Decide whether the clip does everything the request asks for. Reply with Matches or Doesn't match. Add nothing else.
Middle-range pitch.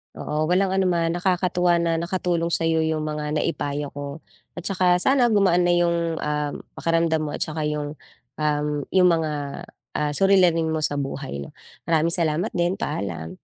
Matches